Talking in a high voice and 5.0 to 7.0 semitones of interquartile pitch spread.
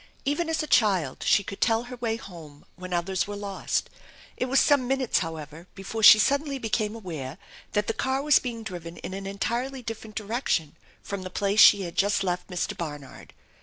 Yes: high, 205 Hz; average, 5.3 semitones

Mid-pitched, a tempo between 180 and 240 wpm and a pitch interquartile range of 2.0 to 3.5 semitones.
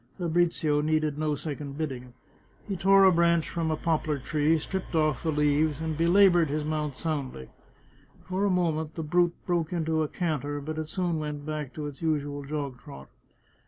Yes: medium, 155 Hz; average, 185 wpm; narrow, 2.4 semitones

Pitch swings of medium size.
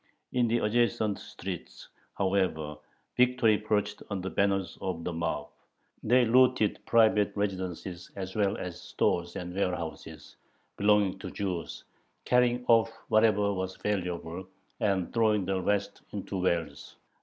Yes: average, 3.0 semitones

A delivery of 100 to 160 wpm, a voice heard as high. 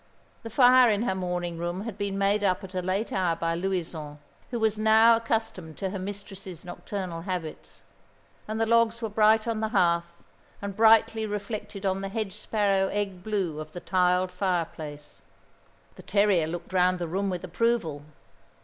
No: average, 175 wpm; high, 195 Hz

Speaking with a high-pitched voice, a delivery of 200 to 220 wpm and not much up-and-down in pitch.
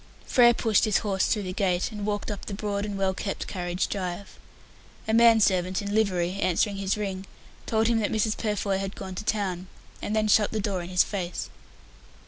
Yes: high, 200 Hz; fast, 205 wpm; narrow, 2.3 semitones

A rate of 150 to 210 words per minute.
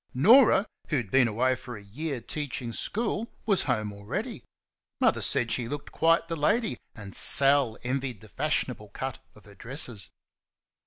Yes: average, 160 wpm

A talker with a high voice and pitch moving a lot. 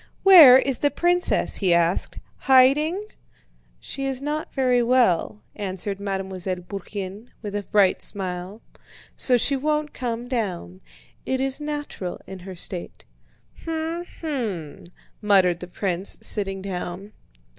Yes: high, 210 Hz; wide, 6.5 semitones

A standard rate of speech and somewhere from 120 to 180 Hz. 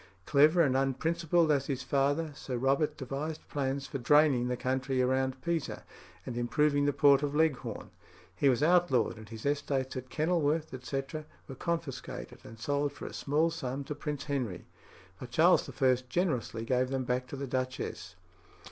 Yes: average, 165 wpm; medium, 140 Hz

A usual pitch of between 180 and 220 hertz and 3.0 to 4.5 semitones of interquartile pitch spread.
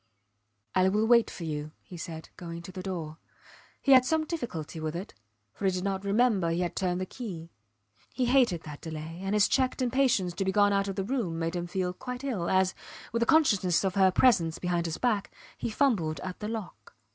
No: high, 190 Hz; average, 5.2 semitones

